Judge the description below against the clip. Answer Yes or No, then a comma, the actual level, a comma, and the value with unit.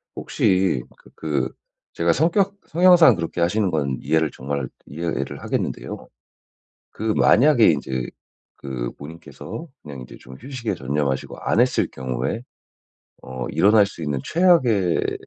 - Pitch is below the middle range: Yes, very low, 85 Hz